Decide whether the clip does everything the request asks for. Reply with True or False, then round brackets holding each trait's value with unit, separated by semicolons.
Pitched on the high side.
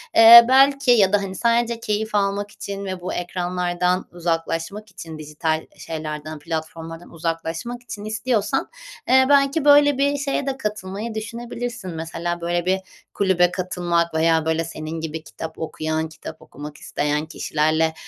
False (180 Hz)